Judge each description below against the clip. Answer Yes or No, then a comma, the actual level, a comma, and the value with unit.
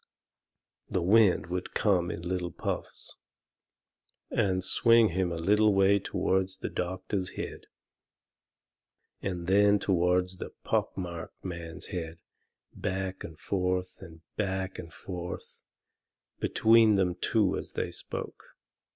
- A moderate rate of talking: No, slow, 120 wpm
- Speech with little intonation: Yes, narrow, 1.9 semitones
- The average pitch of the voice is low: Yes, very low, 95 Hz